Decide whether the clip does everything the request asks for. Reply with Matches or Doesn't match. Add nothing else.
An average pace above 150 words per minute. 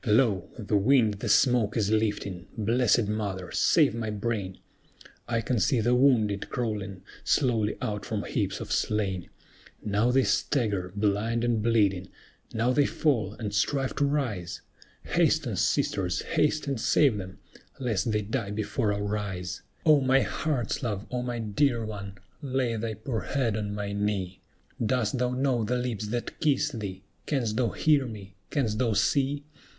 Matches